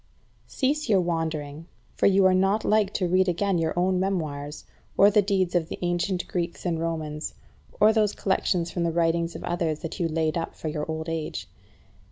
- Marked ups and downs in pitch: No, average, 2.8 semitones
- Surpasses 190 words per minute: Yes, average, 200 wpm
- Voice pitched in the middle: Yes, medium, 175 Hz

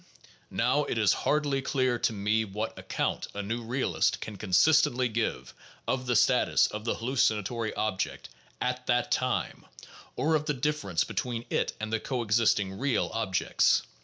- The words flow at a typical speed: Yes, average, 160 wpm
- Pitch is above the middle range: No, low, 115 Hz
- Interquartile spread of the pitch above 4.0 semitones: No, average, 3.3 semitones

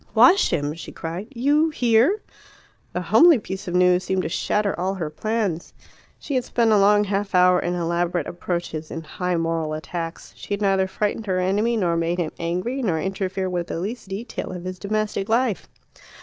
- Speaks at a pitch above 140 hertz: Yes, high, 190 Hz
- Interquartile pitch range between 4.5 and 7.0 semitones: No, average, 3.7 semitones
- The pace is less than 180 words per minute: No, average, 190 wpm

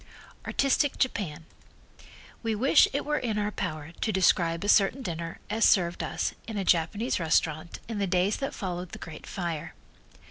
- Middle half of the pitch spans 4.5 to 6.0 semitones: Yes, average, 4.8 semitones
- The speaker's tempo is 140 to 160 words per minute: No, average, 170 wpm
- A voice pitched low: No, high, 190 Hz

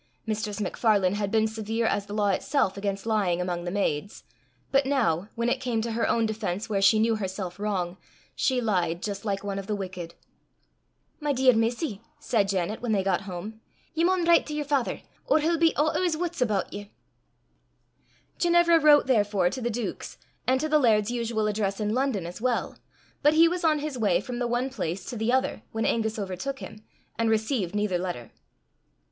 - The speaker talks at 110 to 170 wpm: No, average, 200 wpm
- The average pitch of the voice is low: No, high, 220 Hz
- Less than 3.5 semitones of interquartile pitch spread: No, average, 4.7 semitones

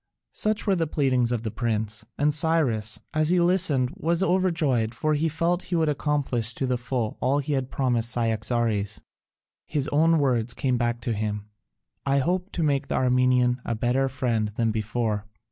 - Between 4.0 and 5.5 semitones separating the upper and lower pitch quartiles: Yes, average, 4.8 semitones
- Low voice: Yes, low, 130 Hz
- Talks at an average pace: Yes, average, 180 wpm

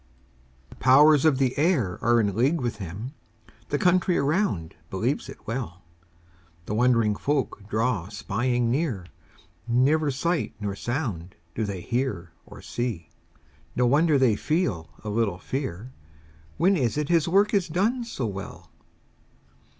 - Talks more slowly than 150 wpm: Yes, average, 140 wpm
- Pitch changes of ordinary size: No, wide, 6.5 semitones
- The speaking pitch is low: Yes, low, 125 Hz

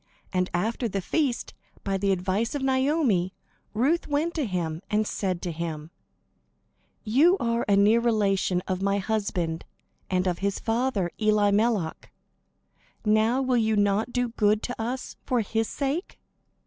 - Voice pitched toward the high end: Yes, high, 215 Hz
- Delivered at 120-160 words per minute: Yes, average, 150 wpm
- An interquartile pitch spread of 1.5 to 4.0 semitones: No, average, 4.4 semitones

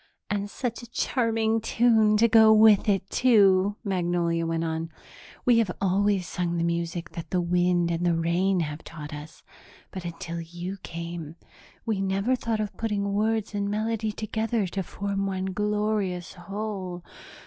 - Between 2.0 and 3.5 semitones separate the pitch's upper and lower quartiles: No, average, 3.9 semitones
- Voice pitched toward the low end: No, high, 195 Hz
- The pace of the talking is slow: No, average, 160 wpm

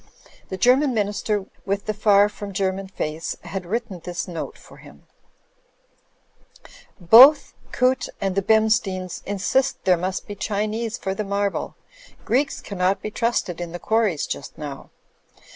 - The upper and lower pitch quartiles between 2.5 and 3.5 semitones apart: Yes, average, 2.9 semitones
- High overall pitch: Yes, high, 200 Hz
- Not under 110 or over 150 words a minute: Yes, average, 145 wpm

